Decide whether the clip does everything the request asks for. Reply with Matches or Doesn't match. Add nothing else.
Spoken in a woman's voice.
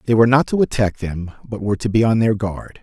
Doesn't match